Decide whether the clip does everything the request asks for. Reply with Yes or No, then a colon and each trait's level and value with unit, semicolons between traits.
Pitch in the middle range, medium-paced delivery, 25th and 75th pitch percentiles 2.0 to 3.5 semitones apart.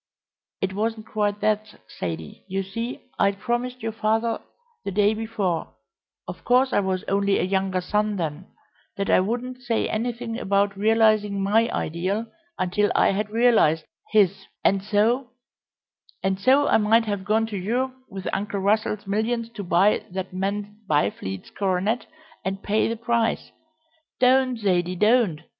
No: high, 210 Hz; average, 155 wpm; average, 2.9 semitones